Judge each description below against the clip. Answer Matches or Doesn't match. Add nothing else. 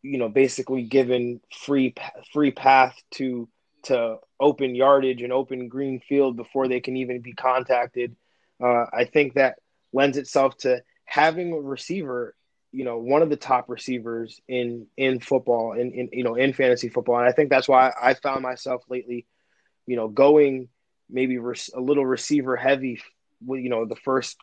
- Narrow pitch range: Matches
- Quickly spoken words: Doesn't match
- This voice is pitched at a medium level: Doesn't match